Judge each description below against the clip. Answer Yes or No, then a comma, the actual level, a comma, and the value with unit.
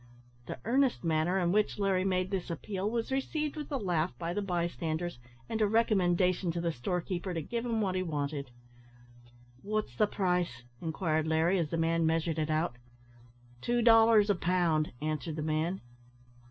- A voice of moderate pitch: Yes, medium, 180 Hz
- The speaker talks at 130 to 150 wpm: No, average, 175 wpm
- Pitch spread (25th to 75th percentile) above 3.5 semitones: Yes, average, 4.4 semitones